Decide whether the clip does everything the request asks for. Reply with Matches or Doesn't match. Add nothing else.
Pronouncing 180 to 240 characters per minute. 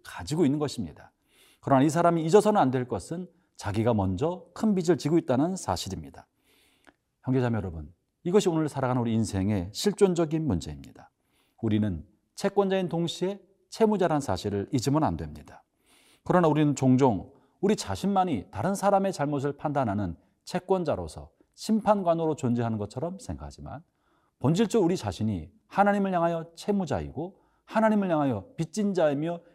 Doesn't match